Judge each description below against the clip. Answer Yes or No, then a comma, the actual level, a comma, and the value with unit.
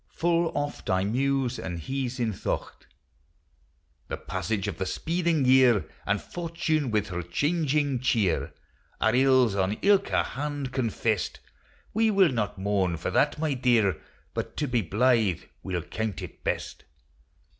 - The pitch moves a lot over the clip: Yes, wide, 6.2 semitones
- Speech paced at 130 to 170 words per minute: Yes, average, 145 wpm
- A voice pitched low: Yes, low, 125 Hz